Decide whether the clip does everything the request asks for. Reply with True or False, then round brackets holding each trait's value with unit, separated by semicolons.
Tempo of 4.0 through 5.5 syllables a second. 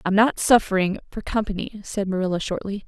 False (6.0 syllables/s)